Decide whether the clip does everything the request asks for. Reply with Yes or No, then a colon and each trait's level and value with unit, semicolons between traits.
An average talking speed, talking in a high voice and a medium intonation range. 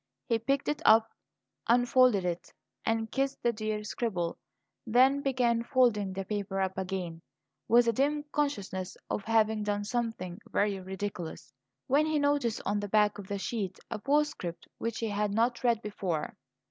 Yes: average, 160 wpm; high, 220 Hz; average, 3.8 semitones